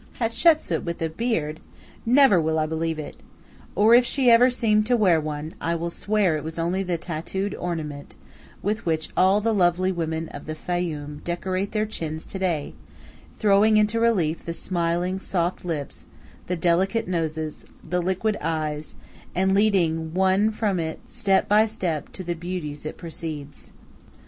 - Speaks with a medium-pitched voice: Yes, medium, 175 Hz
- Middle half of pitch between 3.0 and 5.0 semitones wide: Yes, average, 4.3 semitones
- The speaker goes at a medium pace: Yes, average, 165 wpm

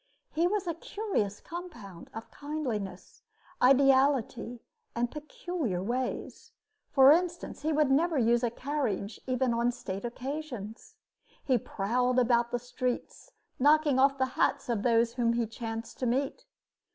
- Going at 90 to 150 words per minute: Yes, average, 140 wpm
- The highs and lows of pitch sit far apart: No, average, 4.0 semitones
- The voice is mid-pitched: No, very high, 250 Hz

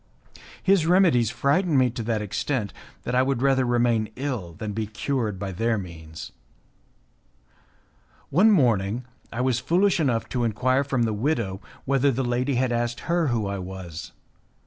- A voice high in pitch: No, low, 120 Hz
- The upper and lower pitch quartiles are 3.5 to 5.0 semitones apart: Yes, average, 4.3 semitones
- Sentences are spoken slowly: No, average, 160 wpm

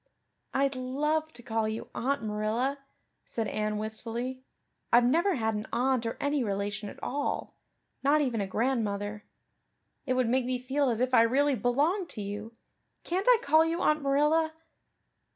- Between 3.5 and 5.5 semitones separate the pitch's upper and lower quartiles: Yes, average, 4.4 semitones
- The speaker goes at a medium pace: Yes, average, 165 wpm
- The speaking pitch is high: Yes, very high, 250 Hz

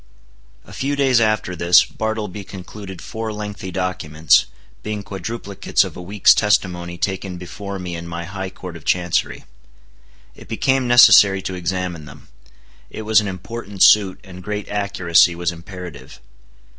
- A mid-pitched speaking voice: No, very low, 95 Hz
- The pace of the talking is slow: No, average, 145 wpm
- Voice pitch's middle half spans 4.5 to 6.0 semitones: No, average, 3.0 semitones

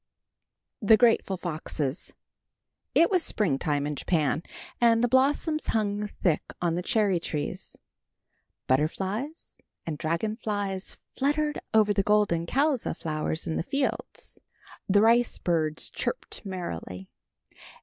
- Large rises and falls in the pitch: Yes, wide, 6.3 semitones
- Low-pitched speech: No, high, 200 Hz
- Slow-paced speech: Yes, slow, 120 wpm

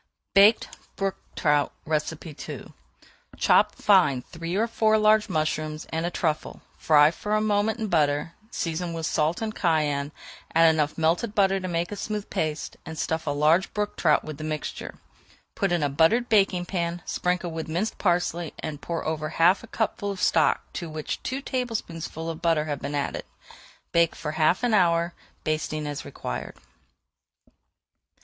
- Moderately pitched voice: Yes, medium, 165 Hz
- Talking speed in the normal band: Yes, average, 165 wpm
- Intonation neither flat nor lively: Yes, average, 4.1 semitones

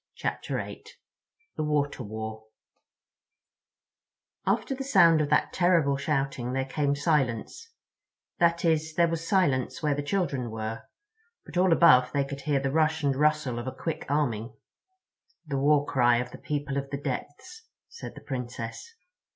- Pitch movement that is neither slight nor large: Yes, average, 3.8 semitones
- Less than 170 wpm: Yes, average, 150 wpm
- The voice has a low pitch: No, medium, 145 Hz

